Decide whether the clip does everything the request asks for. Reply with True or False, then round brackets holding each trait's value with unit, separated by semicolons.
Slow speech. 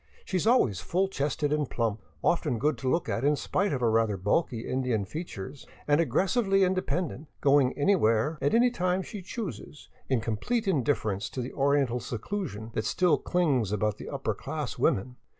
False (185 wpm)